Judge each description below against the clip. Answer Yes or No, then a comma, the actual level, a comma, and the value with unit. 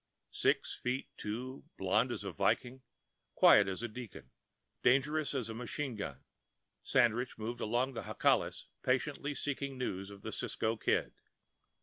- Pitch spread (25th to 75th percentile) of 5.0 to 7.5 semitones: No, average, 3.3 semitones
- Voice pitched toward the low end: Yes, low, 125 Hz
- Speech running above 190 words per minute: No, average, 140 wpm